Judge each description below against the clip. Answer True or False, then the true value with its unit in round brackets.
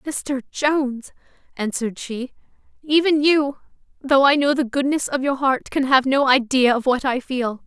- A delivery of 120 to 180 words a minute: True (170 wpm)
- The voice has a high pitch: True (270 Hz)